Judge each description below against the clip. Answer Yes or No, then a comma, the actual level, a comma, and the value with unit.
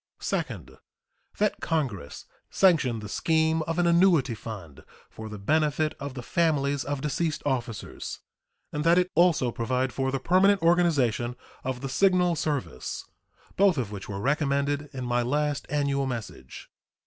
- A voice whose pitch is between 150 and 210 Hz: No, medium, 140 Hz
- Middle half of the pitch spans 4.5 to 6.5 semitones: Yes, average, 4.9 semitones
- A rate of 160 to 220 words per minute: No, average, 150 wpm